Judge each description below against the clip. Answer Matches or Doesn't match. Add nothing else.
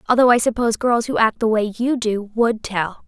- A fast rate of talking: Matches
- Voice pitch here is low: Doesn't match